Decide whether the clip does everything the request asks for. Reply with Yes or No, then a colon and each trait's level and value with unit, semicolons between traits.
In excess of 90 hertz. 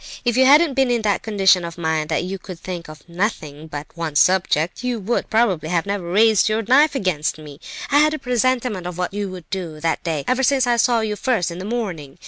Yes: high, 190 Hz